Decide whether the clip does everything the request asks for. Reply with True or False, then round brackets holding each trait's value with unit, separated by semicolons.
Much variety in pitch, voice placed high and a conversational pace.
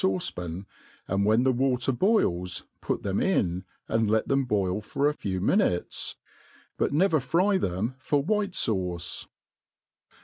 False (8.2 semitones; 115 Hz; 145 wpm)